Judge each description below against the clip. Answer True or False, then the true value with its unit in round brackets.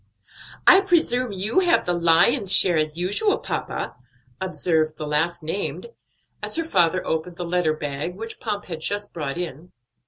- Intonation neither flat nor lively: True (4.7 semitones)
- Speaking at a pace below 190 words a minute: True (160 wpm)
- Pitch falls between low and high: True (180 Hz)